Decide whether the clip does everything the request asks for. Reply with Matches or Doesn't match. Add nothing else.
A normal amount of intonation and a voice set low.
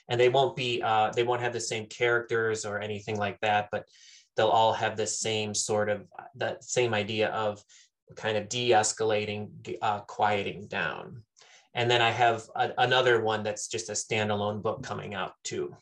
Doesn't match